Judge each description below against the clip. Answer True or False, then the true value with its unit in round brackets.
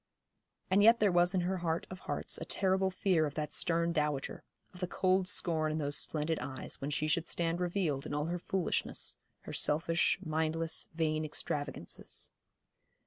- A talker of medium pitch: True (165 Hz)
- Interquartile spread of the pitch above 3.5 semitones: False (3.0 semitones)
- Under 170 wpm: False (175 wpm)